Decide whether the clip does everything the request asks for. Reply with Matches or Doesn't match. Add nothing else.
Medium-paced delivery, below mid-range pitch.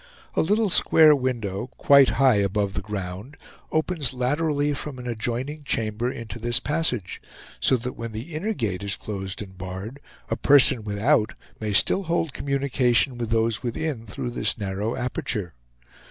Matches